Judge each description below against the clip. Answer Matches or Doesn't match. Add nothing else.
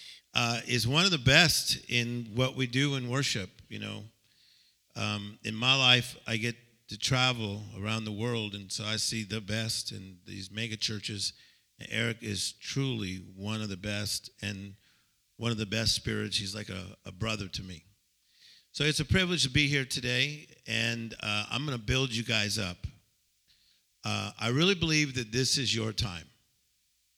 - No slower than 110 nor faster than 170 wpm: Doesn't match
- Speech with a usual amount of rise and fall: Matches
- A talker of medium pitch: Doesn't match